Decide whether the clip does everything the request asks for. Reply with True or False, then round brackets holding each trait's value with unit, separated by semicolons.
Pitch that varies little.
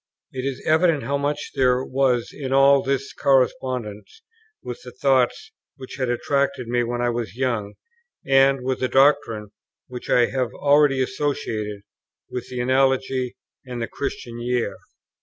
True (2.1 semitones)